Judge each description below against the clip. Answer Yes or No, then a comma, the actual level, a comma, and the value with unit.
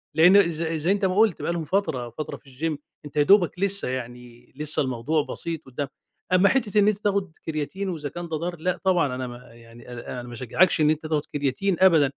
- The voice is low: No, medium, 160 Hz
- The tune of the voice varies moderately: No, wide, 5.9 semitones